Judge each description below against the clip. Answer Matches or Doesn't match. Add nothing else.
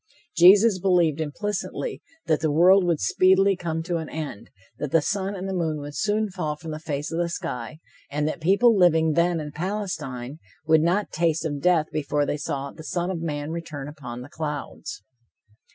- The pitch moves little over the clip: Doesn't match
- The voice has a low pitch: Doesn't match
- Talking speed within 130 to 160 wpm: Doesn't match